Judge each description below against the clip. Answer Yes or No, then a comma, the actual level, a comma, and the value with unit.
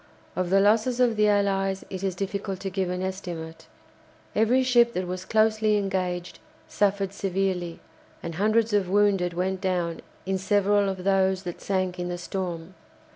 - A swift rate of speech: No, average, 165 wpm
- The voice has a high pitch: Yes, high, 195 Hz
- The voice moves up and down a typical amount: No, narrow, 2.0 semitones